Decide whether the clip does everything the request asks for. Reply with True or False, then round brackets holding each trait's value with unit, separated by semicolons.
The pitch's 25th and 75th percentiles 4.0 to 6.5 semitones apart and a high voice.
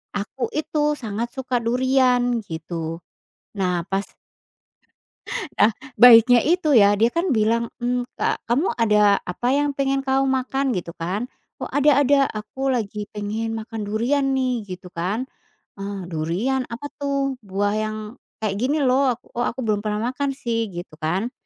True (4.4 semitones; 235 Hz)